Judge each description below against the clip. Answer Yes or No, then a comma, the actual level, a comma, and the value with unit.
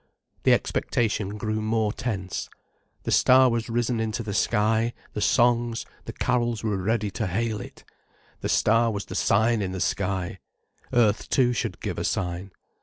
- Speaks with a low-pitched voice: Yes, low, 110 Hz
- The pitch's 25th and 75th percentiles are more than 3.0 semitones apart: No, average, 2.7 semitones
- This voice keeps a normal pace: Yes, average, 165 wpm